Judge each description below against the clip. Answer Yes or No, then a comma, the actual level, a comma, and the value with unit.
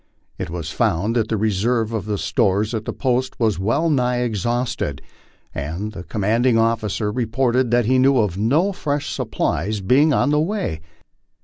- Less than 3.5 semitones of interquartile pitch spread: No, average, 3.8 semitones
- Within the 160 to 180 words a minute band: Yes, average, 165 wpm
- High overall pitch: No, low, 115 Hz